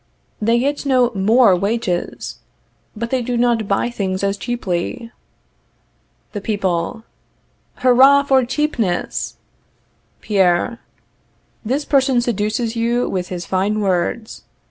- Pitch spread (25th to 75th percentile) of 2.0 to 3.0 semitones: No, average, 3.9 semitones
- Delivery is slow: Yes, slow, 110 wpm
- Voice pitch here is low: No, high, 230 Hz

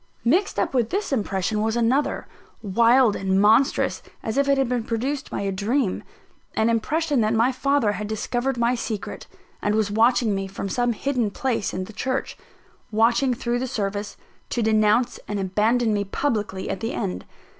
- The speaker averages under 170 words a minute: No, average, 175 wpm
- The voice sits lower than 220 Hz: No, high, 230 Hz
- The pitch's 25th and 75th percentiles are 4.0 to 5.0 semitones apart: No, average, 3.5 semitones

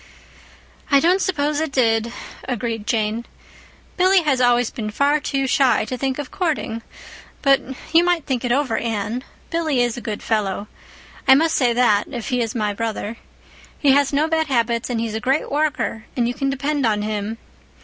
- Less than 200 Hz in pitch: No, very high, 250 Hz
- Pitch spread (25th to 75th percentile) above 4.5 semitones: No, average, 4.2 semitones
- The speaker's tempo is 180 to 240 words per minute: Yes, average, 185 wpm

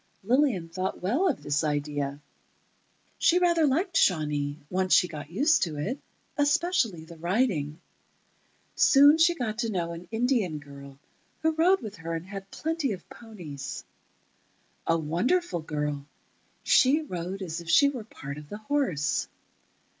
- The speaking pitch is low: No, high, 190 Hz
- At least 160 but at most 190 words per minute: No, average, 145 wpm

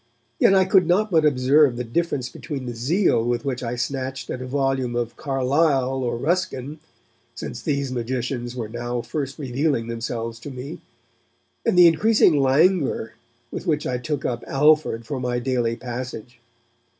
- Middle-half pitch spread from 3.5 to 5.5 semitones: Yes, average, 3.8 semitones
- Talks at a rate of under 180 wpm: Yes, average, 160 wpm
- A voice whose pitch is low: Yes, low, 130 Hz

